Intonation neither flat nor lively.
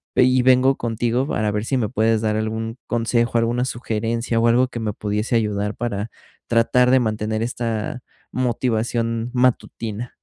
No: narrow, 2.1 semitones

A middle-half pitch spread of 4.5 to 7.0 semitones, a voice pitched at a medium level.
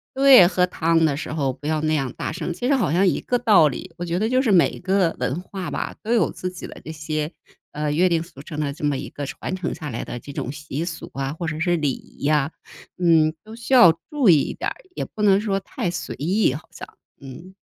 No: average, 4.1 semitones; medium, 165 Hz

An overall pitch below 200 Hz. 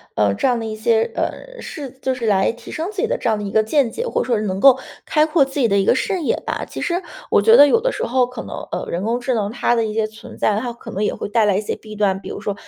No: high, 235 Hz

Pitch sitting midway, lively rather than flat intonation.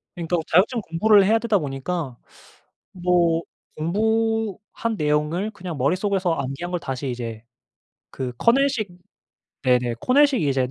Yes: medium, 175 Hz; wide, 7.4 semitones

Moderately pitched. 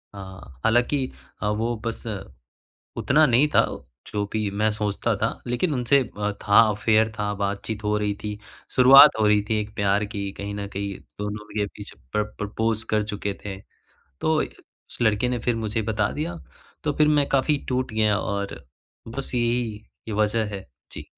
No: low, 110 Hz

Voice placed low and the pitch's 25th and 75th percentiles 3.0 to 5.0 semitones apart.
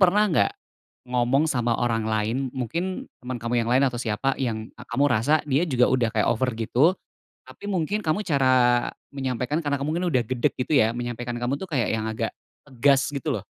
Yes: low, 125 Hz; average, 3.5 semitones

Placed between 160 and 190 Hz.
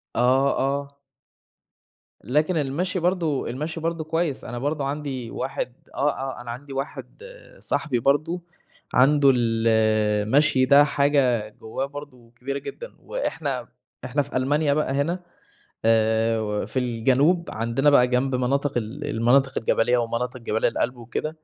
No: low, 135 Hz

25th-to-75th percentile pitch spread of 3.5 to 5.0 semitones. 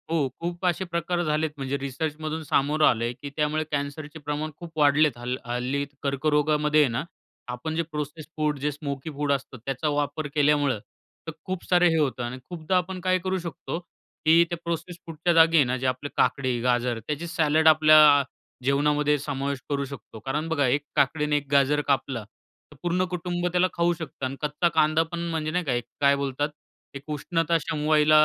No: average, 2.7 semitones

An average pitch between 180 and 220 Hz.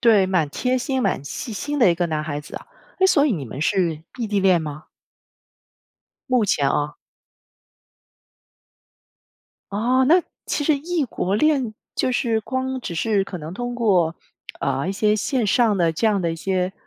Yes: high, 205 Hz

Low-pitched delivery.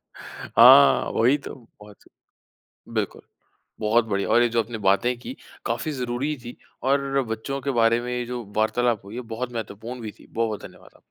Yes: low, 120 Hz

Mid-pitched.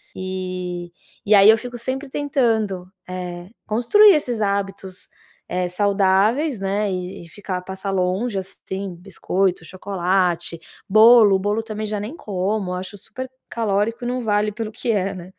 No: high, 200 Hz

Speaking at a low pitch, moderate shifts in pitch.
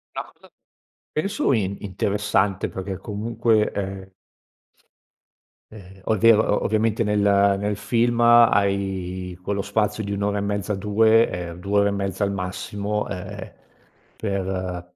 No: low, 100 Hz; narrow, 1.9 semitones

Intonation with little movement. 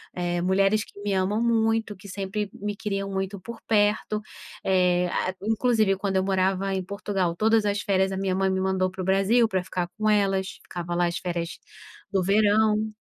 Yes: narrow, 2.0 semitones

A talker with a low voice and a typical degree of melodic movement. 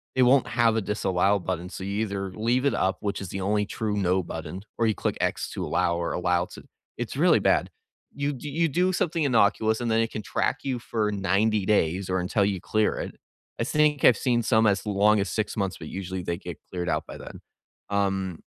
Yes: low, 105 Hz; average, 3.4 semitones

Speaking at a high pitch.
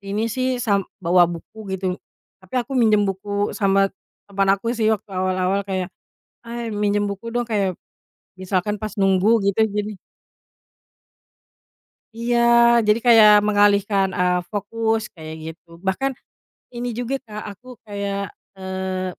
Yes: high, 200 Hz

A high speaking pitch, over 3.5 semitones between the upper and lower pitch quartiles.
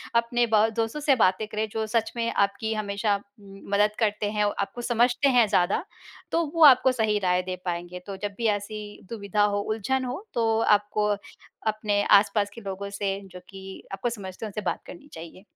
No: high, 210 Hz; narrow, 2.6 semitones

